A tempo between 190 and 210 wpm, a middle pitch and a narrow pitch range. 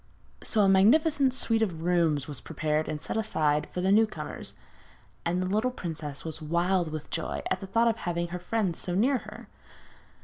No: average, 195 wpm; medium, 180 Hz; wide, 5.4 semitones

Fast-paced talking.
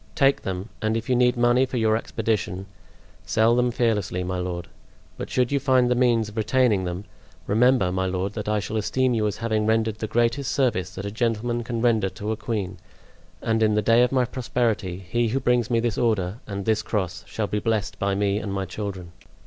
Yes: fast, 215 wpm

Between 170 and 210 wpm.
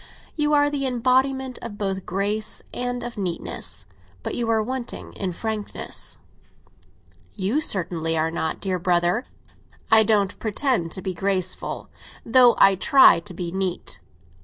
No: average, 140 wpm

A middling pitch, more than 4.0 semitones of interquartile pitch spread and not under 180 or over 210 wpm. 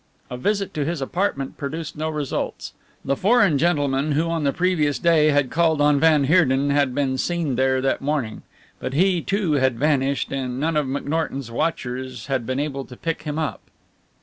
No: medium, 145 Hz; average, 3.3 semitones; average, 185 wpm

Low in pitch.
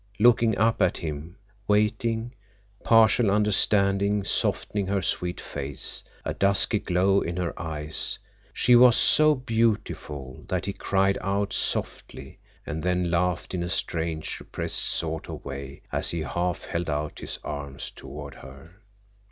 Yes: very low, 90 Hz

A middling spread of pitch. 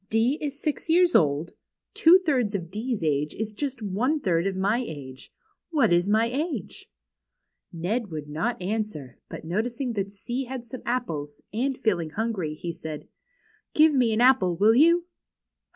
No: wide, 7.0 semitones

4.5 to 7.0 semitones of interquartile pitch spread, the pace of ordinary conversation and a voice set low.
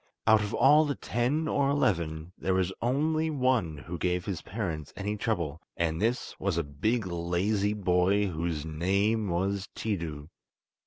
Yes: average, 5.0 semitones; average, 155 wpm; very low, 95 Hz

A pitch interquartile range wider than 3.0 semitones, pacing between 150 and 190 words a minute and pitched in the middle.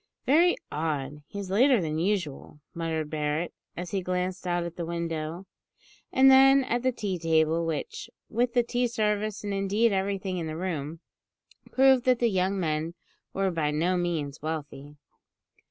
Yes: average, 5.1 semitones; average, 160 wpm; medium, 180 Hz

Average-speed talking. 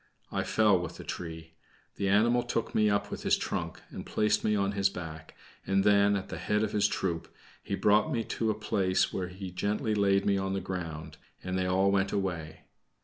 No: fast, 210 wpm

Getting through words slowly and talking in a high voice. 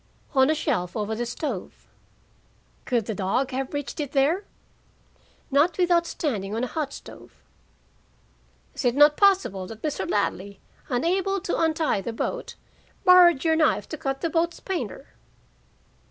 No: average, 150 wpm; very high, 285 Hz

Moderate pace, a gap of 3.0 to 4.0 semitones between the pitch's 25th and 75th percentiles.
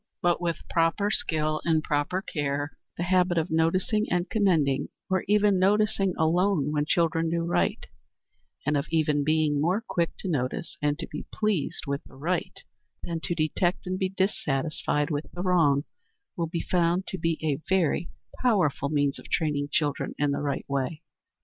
Yes: average, 170 wpm; average, 3.7 semitones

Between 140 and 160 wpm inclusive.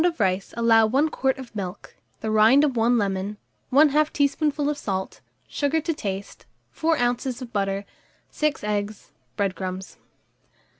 Yes: average, 150 wpm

